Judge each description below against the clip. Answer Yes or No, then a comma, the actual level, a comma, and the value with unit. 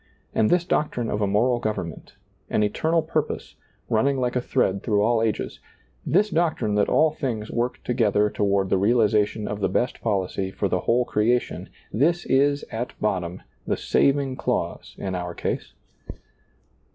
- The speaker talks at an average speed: Yes, average, 165 wpm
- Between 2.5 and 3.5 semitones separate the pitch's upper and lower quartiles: No, average, 4.6 semitones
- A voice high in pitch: No, low, 115 Hz